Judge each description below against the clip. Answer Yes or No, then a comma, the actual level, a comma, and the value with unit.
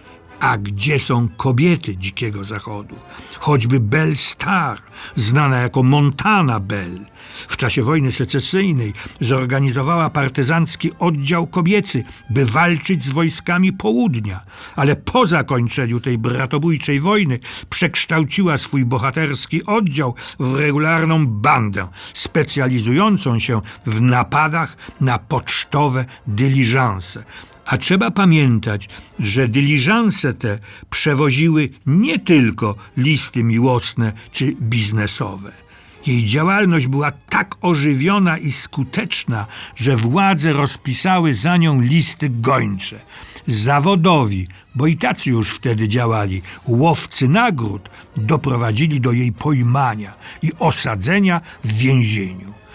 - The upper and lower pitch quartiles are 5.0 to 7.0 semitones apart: Yes, wide, 5.5 semitones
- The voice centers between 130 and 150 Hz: Yes, low, 135 Hz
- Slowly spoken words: Yes, slow, 100 wpm